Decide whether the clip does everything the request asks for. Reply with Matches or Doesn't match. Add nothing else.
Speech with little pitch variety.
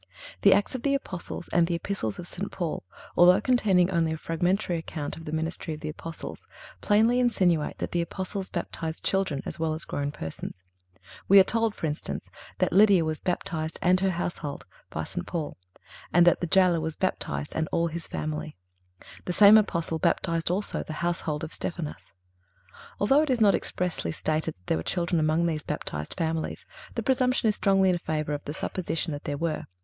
Doesn't match